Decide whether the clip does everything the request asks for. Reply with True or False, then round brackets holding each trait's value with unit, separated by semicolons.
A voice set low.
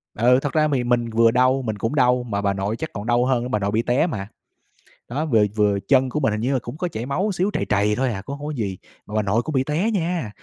True (120 Hz)